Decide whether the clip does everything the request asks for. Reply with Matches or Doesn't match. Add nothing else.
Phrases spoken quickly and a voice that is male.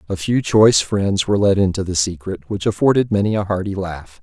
Matches